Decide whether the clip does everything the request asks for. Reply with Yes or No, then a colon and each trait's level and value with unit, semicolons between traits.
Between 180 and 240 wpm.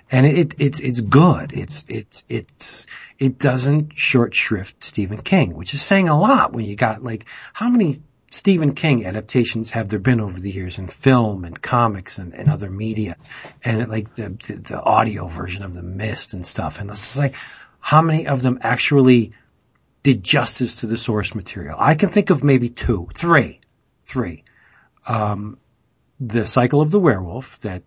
Yes: average, 185 wpm